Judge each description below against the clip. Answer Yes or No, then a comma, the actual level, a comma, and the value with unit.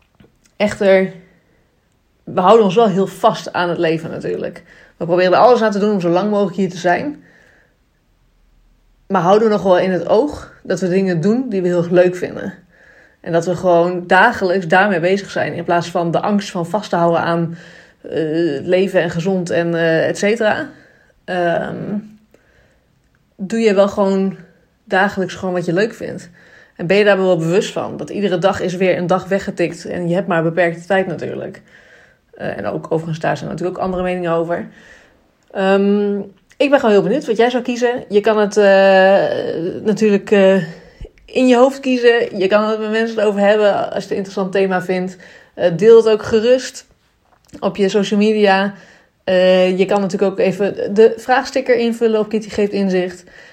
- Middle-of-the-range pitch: No, high, 195 Hz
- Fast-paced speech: No, average, 190 wpm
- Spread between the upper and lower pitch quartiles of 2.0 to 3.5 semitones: Yes, average, 2.9 semitones